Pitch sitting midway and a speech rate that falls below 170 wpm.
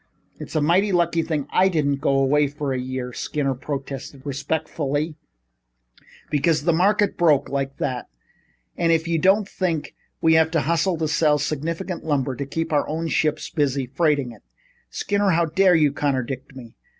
No: medium, 150 Hz; average, 175 wpm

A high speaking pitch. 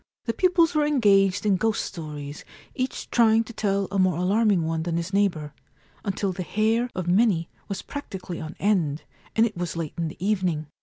Yes: high, 195 Hz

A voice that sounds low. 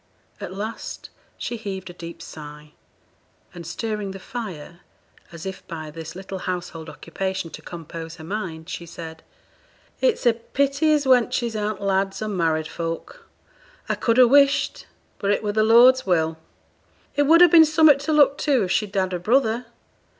No: high, 195 Hz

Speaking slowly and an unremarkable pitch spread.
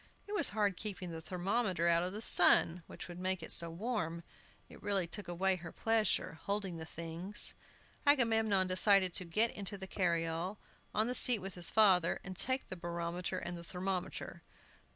No: average, 175 wpm; average, 3.3 semitones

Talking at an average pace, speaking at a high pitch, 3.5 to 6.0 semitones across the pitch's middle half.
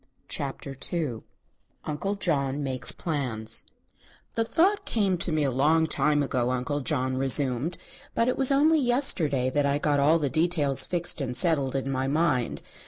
No: average, 165 wpm; medium, 145 Hz; average, 4.3 semitones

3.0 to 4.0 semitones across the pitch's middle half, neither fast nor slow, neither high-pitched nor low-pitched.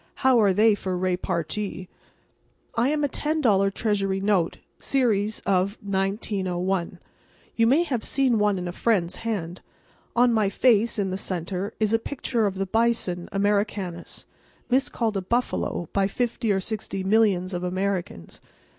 No: average, 3.4 semitones; average, 150 wpm; high, 200 Hz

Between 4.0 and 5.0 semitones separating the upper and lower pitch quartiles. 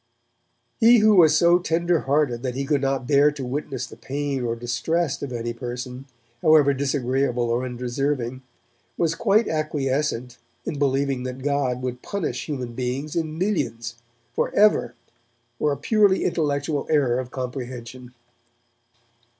No: average, 3.6 semitones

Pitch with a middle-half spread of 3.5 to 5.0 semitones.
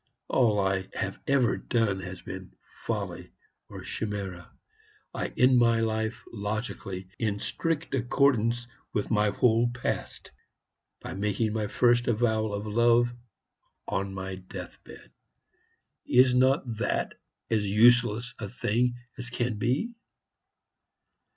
No: average, 2.8 semitones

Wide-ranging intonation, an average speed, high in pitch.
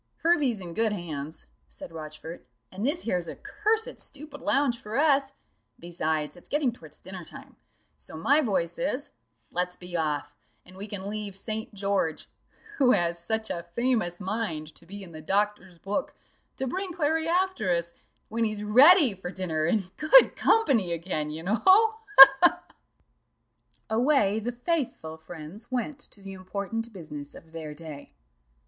Yes: wide, 7.5 semitones; average, 160 wpm; high, 200 Hz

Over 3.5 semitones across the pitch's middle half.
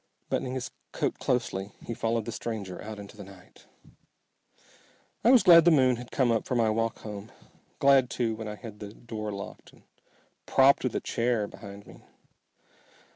No: average, 3.2 semitones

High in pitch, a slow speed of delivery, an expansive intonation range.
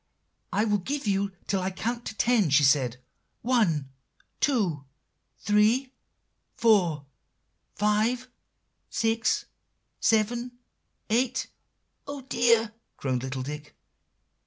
Yes: high, 210 Hz; slow, 100 wpm; wide, 7.3 semitones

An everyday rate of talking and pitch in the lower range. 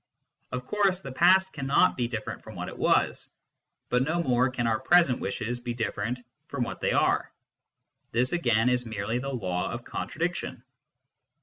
Yes: average, 170 wpm; low, 125 Hz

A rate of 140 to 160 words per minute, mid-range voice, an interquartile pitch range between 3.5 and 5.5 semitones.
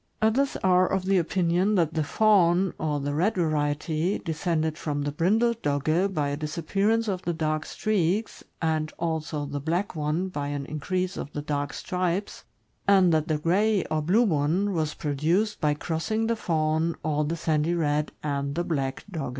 No: average, 175 wpm; medium, 165 Hz; average, 3.9 semitones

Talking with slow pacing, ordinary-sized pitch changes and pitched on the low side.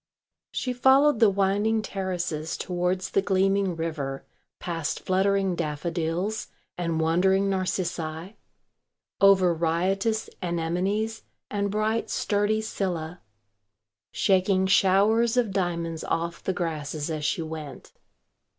No: slow, 105 wpm; average, 3.3 semitones; medium, 185 Hz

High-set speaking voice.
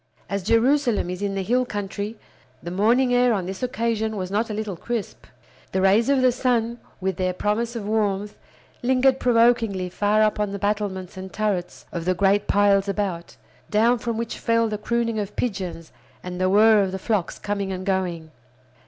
Yes: high, 210 Hz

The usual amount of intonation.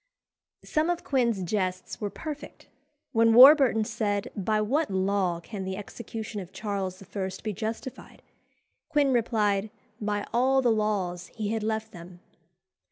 Yes: average, 3.3 semitones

